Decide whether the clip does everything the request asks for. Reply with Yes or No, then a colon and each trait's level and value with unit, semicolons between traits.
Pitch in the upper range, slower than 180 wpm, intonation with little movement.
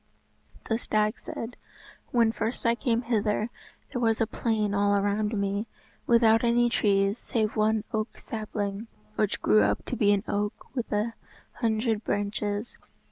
Yes: high, 215 Hz; average, 150 wpm; narrow, 2.1 semitones